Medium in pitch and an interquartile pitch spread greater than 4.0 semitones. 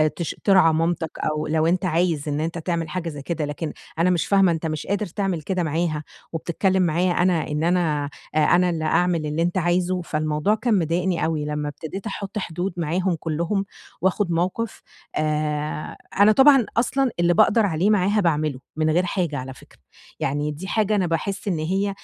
No: medium, 170 Hz; average, 3.3 semitones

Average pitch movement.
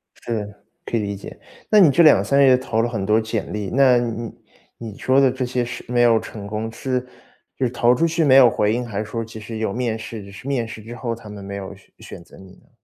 Yes: average, 3.0 semitones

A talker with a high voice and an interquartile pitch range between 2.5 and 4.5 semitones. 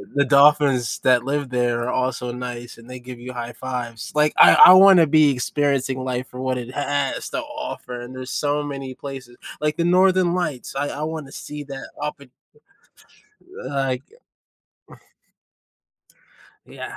No: low, 135 Hz; average, 2.9 semitones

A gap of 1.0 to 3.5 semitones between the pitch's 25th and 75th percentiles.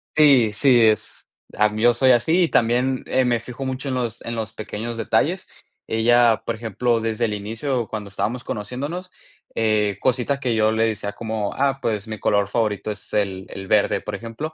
Yes: average, 2.8 semitones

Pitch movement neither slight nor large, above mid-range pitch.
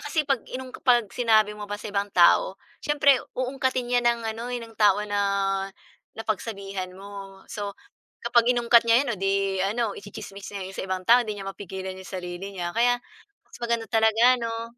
Yes: average, 3.6 semitones; high, 220 Hz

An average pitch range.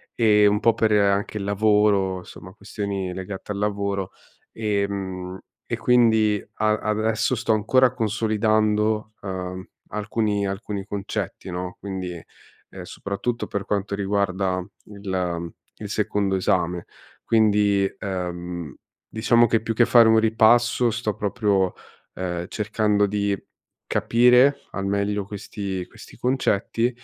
No: narrow, 2.2 semitones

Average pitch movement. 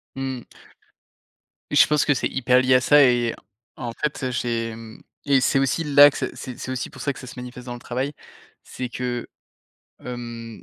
No: narrow, 1.9 semitones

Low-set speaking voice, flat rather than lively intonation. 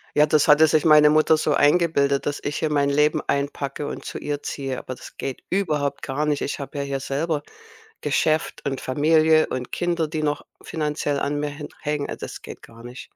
No: medium, 145 Hz; narrow, 1.7 semitones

